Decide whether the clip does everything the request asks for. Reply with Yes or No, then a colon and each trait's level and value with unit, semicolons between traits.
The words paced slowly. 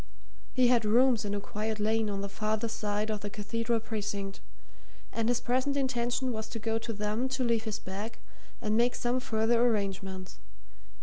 No: average, 180 wpm